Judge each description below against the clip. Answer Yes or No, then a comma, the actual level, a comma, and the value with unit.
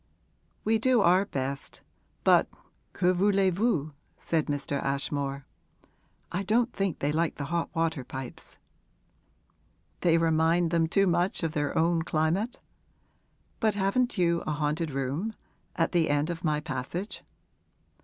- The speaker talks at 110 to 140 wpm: Yes, slow, 135 wpm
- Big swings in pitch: No, average, 4.4 semitones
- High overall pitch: No, medium, 165 Hz